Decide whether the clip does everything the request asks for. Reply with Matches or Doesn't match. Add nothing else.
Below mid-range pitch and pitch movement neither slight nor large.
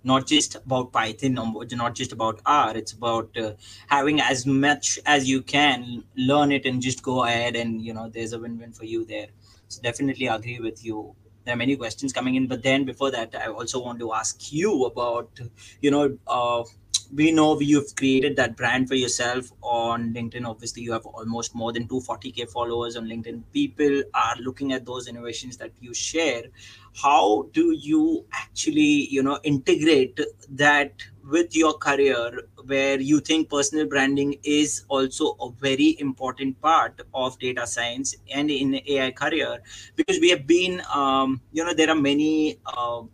Matches